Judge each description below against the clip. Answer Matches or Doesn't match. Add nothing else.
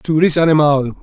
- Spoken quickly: Doesn't match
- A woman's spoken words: Doesn't match